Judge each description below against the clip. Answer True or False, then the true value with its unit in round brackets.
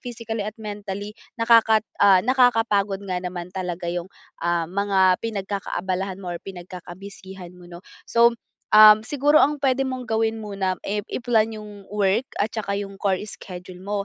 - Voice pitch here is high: True (200 Hz)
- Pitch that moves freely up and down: False (3.1 semitones)